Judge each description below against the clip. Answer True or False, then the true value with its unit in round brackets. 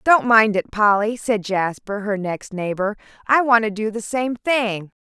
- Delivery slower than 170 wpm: False (190 wpm)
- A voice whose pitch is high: True (215 Hz)